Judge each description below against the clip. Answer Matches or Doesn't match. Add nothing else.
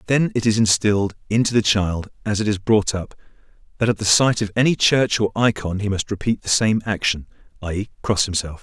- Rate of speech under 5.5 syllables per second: Doesn't match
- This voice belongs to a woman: Doesn't match